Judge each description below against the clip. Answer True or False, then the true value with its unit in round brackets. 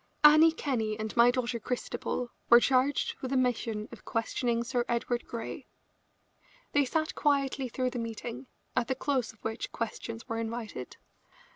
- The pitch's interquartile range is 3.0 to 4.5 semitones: False (2.4 semitones)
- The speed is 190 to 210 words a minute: False (155 wpm)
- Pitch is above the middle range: True (245 Hz)